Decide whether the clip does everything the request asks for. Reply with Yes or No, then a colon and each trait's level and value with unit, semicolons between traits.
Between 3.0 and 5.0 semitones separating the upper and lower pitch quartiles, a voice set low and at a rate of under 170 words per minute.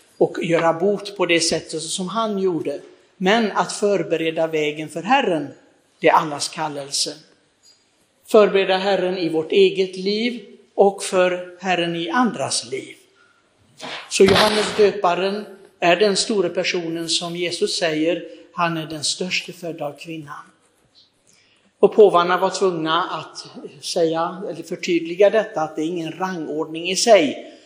No: average, 3.5 semitones; medium, 180 Hz; average, 140 wpm